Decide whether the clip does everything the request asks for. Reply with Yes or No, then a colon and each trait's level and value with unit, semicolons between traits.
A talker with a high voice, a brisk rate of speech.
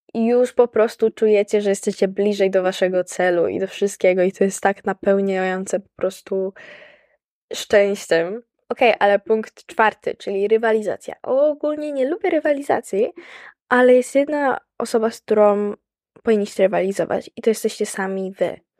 No: high, 210 Hz; average, 150 wpm